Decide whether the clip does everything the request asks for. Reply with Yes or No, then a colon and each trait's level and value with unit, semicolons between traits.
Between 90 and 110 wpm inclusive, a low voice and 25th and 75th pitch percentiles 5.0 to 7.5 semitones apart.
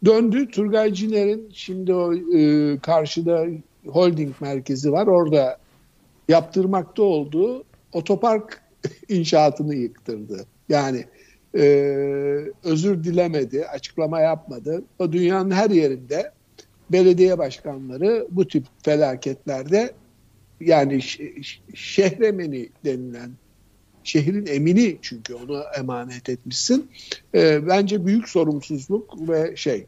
No: slow, 95 wpm; medium, 160 Hz; wide, 5.6 semitones